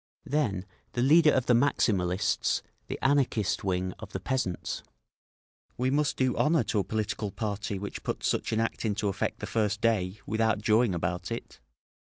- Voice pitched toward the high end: No, low, 110 Hz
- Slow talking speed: No, average, 170 wpm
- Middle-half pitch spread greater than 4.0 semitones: Yes, average, 4.4 semitones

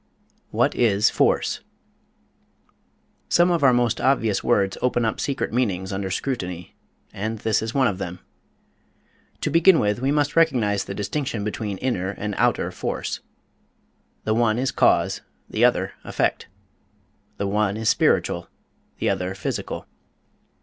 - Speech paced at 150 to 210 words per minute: No, average, 140 wpm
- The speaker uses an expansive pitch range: No, average, 4.5 semitones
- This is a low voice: Yes, low, 110 Hz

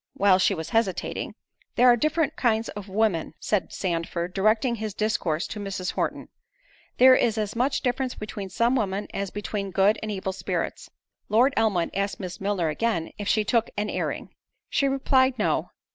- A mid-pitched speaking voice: No, high, 210 Hz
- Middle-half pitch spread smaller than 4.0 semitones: Yes, average, 3.4 semitones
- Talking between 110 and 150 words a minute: No, average, 170 wpm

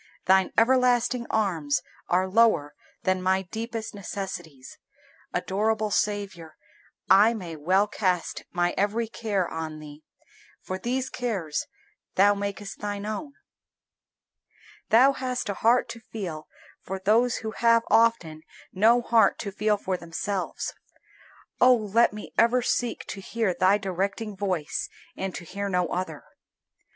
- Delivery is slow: Yes, slow, 130 wpm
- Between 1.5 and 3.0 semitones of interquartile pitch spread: No, average, 3.7 semitones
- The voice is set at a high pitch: Yes, high, 200 Hz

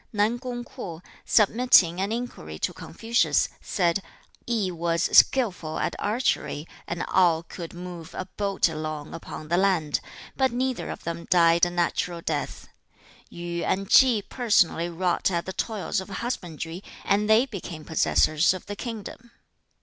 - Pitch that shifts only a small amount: No, average, 4.6 semitones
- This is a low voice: No, medium, 180 Hz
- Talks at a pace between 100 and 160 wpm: Yes, average, 150 wpm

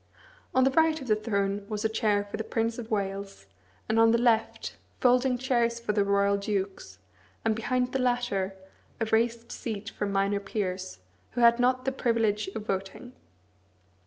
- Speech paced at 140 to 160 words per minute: No, average, 175 wpm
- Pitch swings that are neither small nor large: Yes, average, 3.3 semitones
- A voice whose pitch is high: Yes, high, 220 Hz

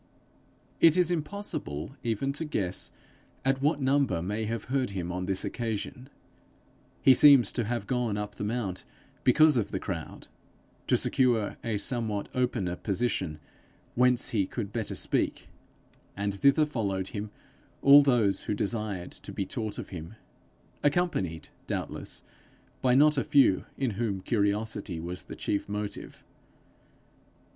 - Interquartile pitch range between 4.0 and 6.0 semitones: Yes, average, 5.0 semitones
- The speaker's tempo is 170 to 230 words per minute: No, average, 140 wpm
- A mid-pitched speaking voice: No, low, 115 Hz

